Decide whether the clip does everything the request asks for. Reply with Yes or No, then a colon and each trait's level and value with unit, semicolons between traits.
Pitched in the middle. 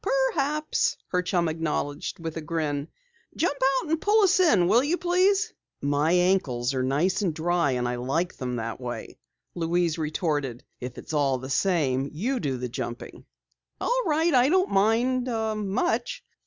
Yes: medium, 170 Hz